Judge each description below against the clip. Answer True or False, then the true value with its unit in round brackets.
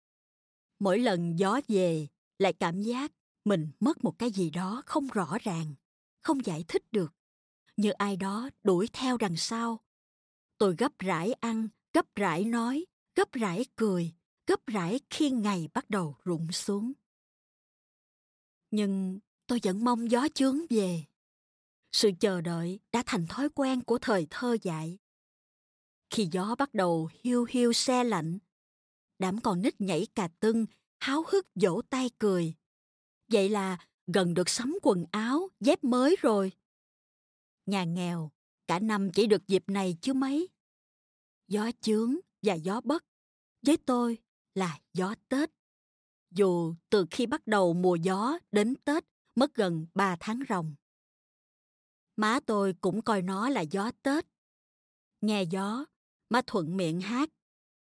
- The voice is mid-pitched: False (210 Hz)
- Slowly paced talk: True (145 wpm)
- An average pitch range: True (4.9 semitones)